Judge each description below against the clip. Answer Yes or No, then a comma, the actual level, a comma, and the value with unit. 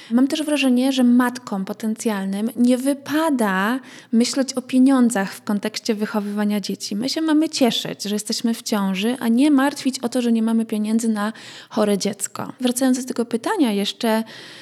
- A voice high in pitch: Yes, high, 235 Hz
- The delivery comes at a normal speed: No, fast, 165 wpm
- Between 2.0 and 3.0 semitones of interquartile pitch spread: No, average, 3.4 semitones